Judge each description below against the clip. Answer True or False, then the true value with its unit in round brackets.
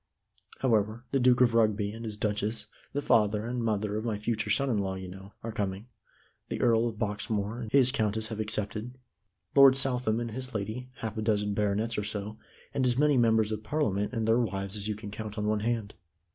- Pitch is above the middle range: False (110 Hz)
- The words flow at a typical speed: False (215 wpm)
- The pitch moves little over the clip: True (2.2 semitones)